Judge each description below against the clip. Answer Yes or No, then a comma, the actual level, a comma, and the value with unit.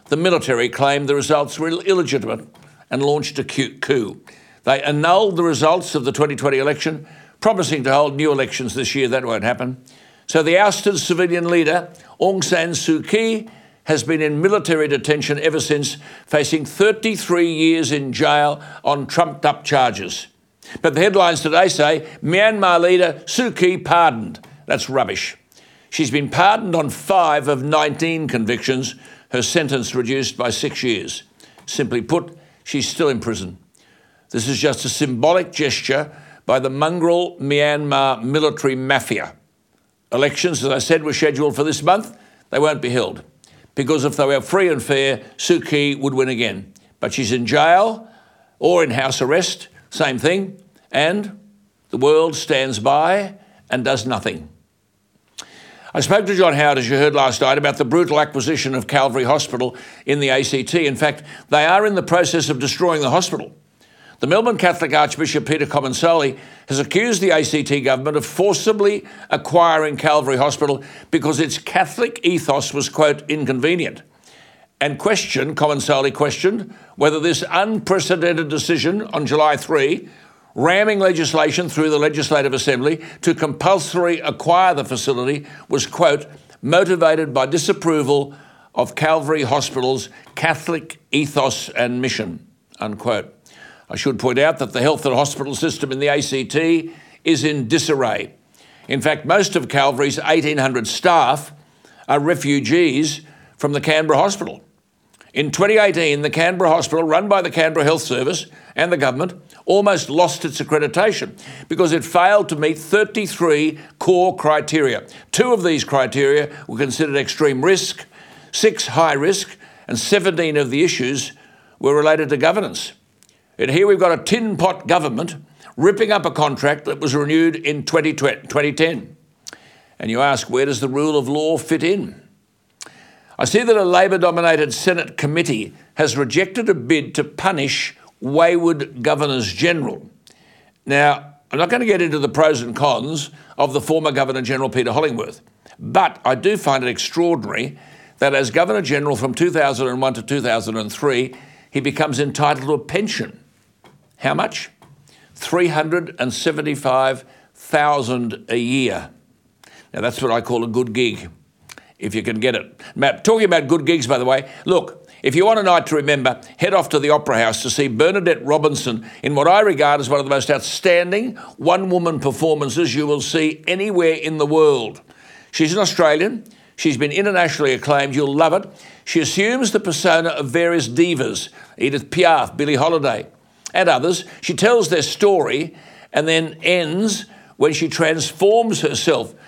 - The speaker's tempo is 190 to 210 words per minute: No, average, 150 wpm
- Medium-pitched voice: Yes, medium, 155 Hz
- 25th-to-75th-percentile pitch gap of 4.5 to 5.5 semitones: No, average, 3.6 semitones